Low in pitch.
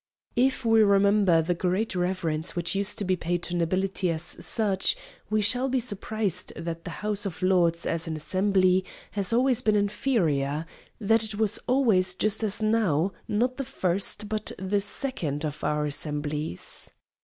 No: high, 195 Hz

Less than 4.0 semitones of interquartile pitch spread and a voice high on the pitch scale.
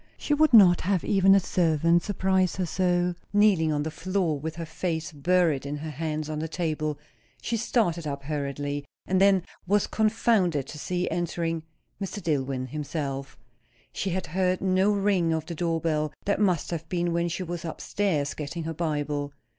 No: average, 3.6 semitones; medium, 170 Hz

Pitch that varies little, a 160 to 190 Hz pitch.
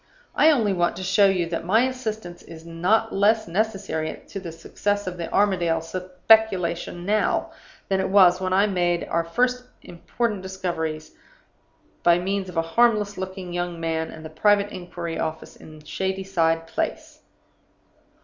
No: average, 3.3 semitones; medium, 185 Hz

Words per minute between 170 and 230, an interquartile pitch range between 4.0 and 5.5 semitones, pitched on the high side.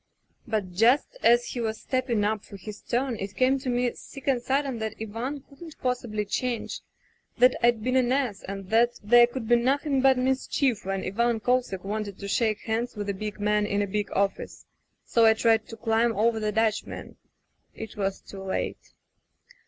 No: average, 190 wpm; average, 3.2 semitones; high, 225 Hz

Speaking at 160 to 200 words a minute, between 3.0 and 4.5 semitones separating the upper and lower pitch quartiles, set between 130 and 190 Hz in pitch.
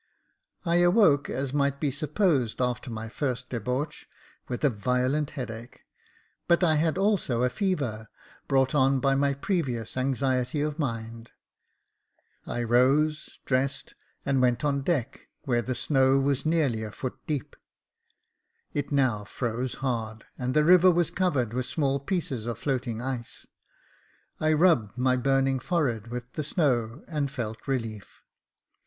No: average, 145 wpm; average, 3.7 semitones; low, 135 Hz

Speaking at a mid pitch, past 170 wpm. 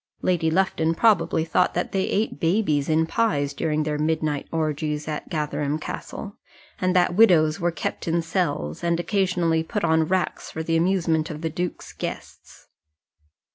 No: medium, 165 Hz; average, 160 wpm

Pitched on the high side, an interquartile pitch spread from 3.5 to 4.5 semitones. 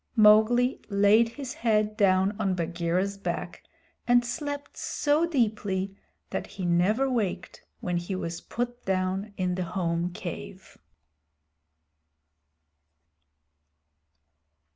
Yes: high, 200 Hz; average, 4.2 semitones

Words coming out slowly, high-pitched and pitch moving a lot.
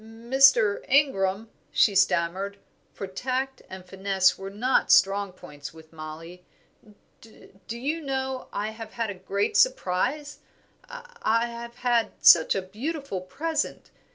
Yes: slow, 125 wpm; high, 220 Hz; wide, 5.7 semitones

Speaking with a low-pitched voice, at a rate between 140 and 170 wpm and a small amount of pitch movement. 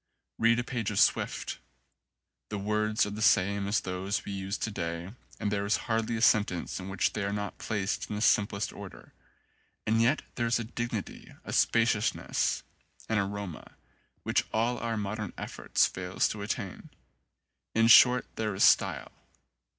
Yes: low, 105 Hz; average, 165 wpm; narrow, 2.3 semitones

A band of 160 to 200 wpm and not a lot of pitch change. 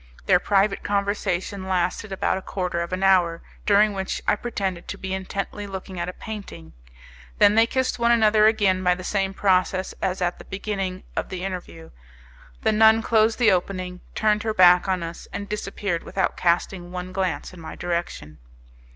Yes: average, 180 wpm; narrow, 2.3 semitones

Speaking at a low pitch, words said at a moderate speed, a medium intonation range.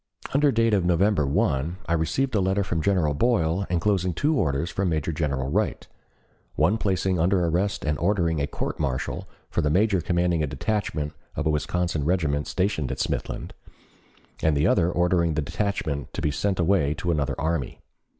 Yes: very low, 85 Hz; average, 180 wpm; average, 4.5 semitones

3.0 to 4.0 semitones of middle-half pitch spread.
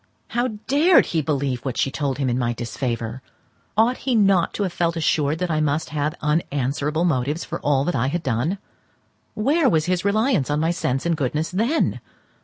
No: average, 5.1 semitones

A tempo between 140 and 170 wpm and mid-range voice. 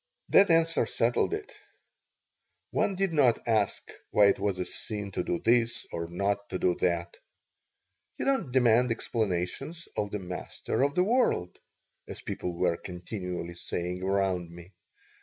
No: average, 150 wpm; low, 100 Hz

